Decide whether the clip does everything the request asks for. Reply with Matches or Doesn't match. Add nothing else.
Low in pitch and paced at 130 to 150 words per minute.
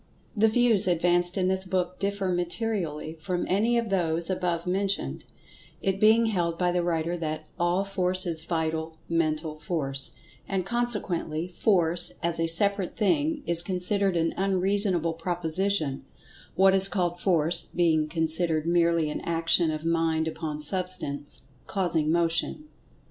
Doesn't match